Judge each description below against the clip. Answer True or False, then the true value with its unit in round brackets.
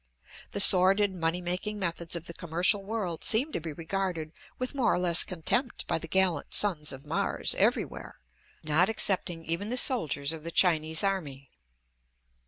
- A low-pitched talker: False (175 Hz)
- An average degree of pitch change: True (3.5 semitones)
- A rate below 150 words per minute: False (165 wpm)